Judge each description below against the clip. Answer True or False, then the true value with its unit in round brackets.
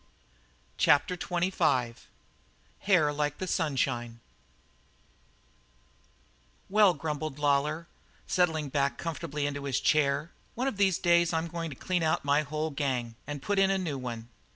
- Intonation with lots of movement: False (3.5 semitones)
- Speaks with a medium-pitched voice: True (150 Hz)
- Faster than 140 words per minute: False (135 wpm)